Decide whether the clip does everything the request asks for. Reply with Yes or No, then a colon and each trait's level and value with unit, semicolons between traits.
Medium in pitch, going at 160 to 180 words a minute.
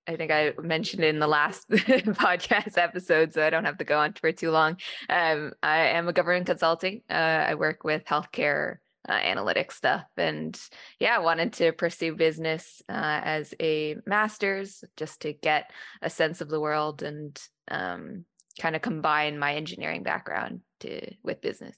Yes: medium, 160 Hz; average, 175 wpm